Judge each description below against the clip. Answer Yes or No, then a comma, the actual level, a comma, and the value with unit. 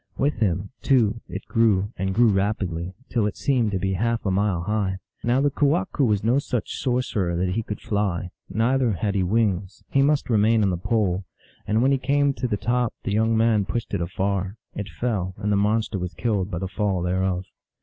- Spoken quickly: Yes, fast, 210 wpm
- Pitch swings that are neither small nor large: Yes, average, 3.6 semitones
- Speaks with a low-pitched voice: Yes, low, 105 Hz